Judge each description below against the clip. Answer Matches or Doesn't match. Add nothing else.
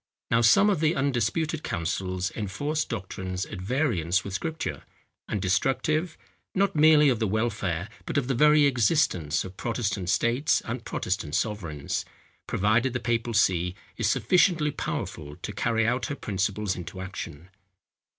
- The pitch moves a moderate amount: Doesn't match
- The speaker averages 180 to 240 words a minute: Doesn't match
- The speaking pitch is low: Matches